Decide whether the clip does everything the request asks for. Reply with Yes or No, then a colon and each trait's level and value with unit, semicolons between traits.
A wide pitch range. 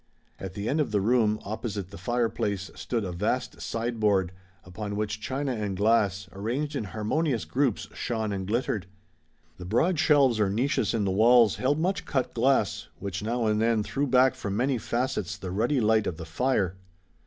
No: average, 4.0 semitones